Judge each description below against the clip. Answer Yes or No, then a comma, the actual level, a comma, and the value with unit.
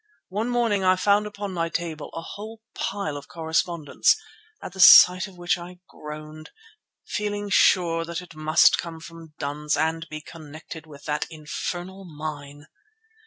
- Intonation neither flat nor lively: Yes, average, 3.4 semitones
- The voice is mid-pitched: Yes, medium, 165 Hz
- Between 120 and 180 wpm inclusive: Yes, average, 155 wpm